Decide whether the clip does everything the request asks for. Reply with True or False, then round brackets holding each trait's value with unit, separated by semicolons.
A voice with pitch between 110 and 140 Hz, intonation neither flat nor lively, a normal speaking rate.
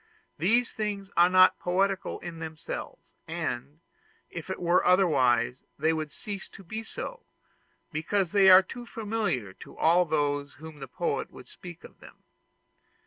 False (175 Hz; 4.4 semitones; 155 wpm)